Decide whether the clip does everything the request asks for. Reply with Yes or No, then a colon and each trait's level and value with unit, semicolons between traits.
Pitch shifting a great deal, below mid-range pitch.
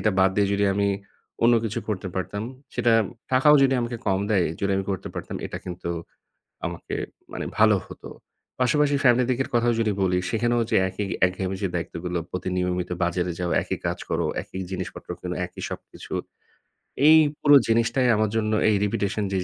No: average, 4.3 semitones; low, 105 Hz